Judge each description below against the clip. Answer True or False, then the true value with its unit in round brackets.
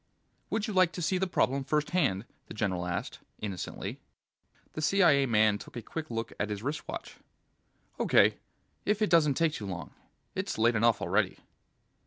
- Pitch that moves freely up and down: True (7.8 semitones)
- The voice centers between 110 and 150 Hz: True (135 Hz)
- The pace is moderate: True (170 wpm)